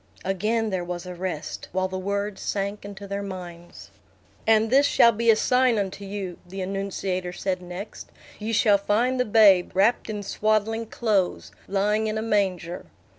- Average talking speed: Yes, average, 170 wpm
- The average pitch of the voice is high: Yes, high, 200 Hz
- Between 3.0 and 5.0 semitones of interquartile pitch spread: No, narrow, 2.6 semitones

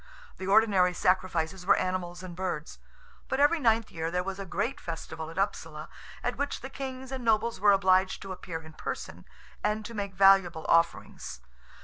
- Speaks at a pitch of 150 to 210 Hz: Yes, high, 190 Hz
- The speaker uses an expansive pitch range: No, average, 4.1 semitones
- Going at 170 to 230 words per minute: Yes, average, 175 wpm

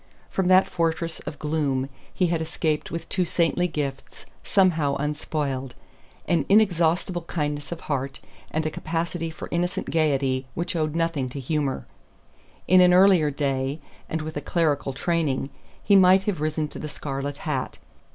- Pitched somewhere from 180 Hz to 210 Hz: No, medium, 155 Hz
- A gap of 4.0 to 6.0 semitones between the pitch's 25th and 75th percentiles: No, average, 3.2 semitones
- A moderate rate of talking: Yes, average, 155 wpm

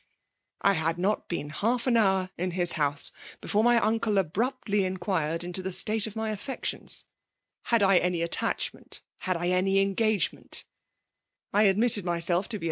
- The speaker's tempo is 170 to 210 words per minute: Yes, average, 185 wpm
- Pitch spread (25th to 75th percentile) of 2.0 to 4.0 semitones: Yes, average, 3.6 semitones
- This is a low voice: No, high, 195 Hz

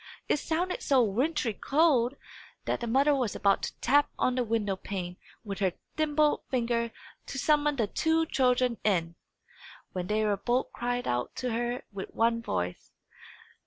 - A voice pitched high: Yes, high, 240 Hz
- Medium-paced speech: Yes, average, 160 wpm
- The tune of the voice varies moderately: Yes, average, 4.9 semitones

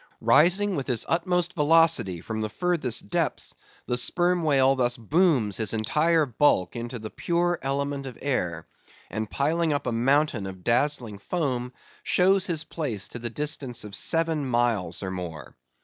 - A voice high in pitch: No, low, 135 Hz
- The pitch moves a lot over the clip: Yes, wide, 6.5 semitones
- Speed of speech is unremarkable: Yes, average, 160 wpm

